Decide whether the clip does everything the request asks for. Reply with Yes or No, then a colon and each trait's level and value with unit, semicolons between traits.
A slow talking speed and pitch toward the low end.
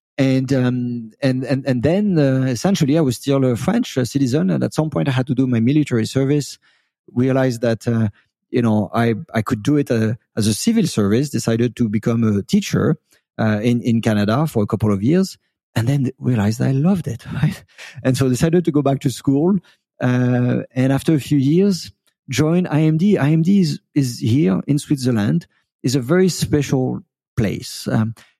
No: average, 190 wpm; low, 130 Hz